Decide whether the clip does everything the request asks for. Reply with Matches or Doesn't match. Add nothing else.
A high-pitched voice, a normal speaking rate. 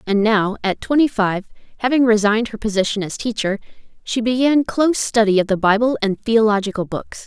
Matches